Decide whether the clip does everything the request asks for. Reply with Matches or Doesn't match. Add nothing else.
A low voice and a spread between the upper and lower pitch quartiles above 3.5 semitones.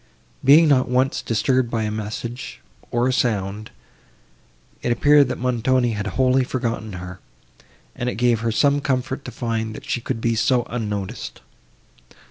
Doesn't match